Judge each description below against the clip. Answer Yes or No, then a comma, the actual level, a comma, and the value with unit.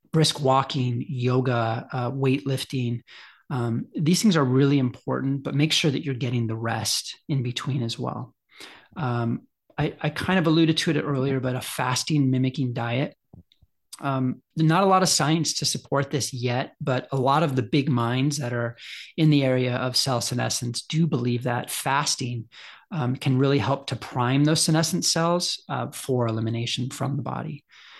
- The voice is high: No, low, 135 Hz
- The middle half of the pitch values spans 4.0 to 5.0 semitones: No, average, 3.1 semitones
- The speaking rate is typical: Yes, average, 175 wpm